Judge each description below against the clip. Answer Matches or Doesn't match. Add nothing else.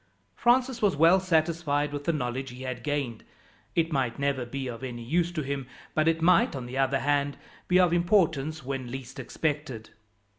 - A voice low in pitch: Doesn't match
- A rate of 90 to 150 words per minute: Doesn't match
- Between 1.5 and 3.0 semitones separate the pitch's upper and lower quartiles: Doesn't match